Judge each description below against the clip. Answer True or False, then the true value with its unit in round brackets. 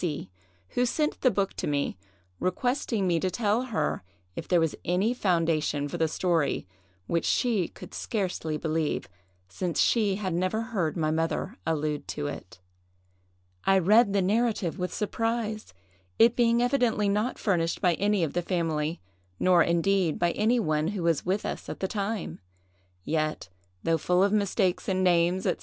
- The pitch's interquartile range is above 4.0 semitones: True (4.5 semitones)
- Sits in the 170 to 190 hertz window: True (185 Hz)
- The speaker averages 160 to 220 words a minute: True (165 wpm)